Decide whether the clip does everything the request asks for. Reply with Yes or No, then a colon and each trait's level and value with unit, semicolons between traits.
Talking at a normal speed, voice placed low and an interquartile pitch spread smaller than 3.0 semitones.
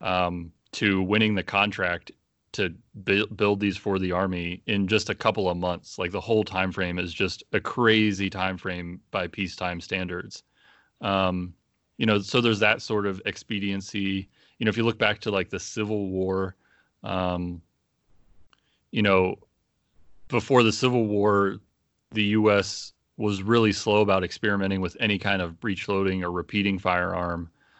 Yes: average, 160 wpm; low, 100 Hz; narrow, 2.5 semitones